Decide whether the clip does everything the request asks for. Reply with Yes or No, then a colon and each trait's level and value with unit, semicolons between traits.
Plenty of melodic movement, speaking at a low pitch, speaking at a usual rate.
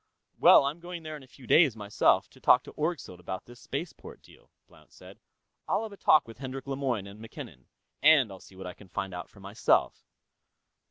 No: wide, 7.3 semitones; low, 125 Hz; fast, 210 wpm